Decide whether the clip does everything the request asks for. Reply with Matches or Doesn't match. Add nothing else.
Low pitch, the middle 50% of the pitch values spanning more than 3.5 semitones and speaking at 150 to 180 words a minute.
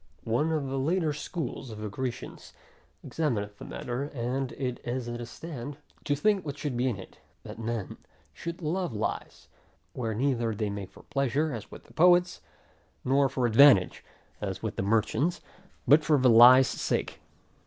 Matches